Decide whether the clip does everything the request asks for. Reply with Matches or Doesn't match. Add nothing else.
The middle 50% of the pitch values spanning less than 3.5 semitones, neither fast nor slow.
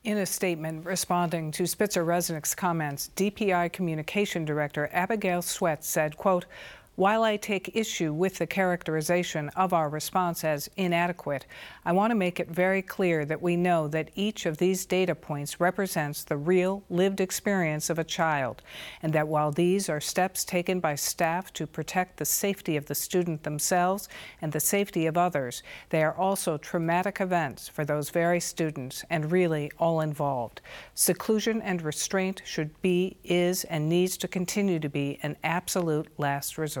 Matches